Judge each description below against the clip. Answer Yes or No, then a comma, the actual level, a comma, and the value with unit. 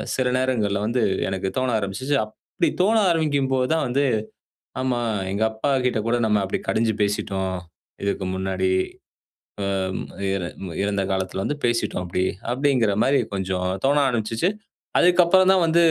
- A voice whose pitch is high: No, low, 115 Hz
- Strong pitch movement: Yes, wide, 6.4 semitones